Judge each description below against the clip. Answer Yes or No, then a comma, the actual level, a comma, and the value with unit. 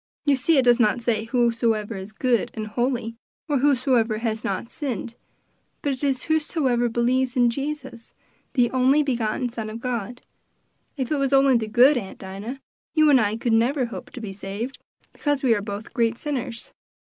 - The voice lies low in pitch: No, high, 240 Hz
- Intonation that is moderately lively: Yes, average, 3.1 semitones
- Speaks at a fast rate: No, average, 180 wpm